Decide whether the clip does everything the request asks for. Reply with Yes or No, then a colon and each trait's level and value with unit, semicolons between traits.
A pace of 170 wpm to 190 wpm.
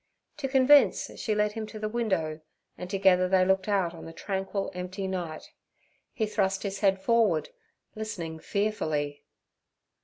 No: average, 150 wpm